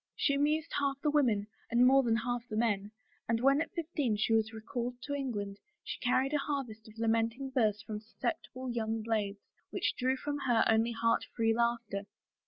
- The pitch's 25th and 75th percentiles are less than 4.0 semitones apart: Yes, average, 3.6 semitones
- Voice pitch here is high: Yes, high, 235 Hz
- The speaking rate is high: No, average, 190 wpm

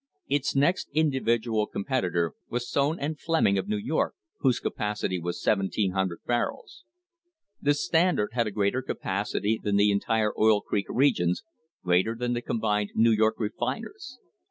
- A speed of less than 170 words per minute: Yes, average, 150 wpm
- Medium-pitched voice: No, low, 110 Hz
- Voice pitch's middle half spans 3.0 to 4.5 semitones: No, average, 5.2 semitones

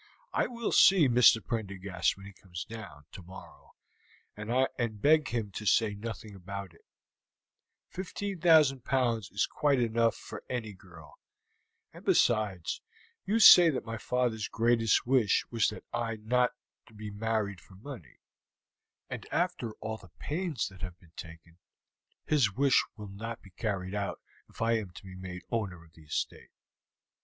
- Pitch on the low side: Yes, low, 110 Hz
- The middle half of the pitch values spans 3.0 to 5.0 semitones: Yes, average, 4.4 semitones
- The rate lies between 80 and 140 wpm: No, average, 155 wpm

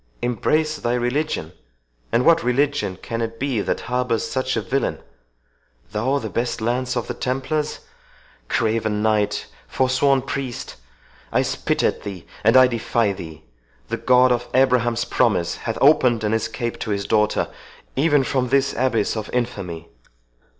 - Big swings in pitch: No, average, 3.5 semitones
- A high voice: No, low, 120 Hz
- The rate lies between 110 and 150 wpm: Yes, slow, 135 wpm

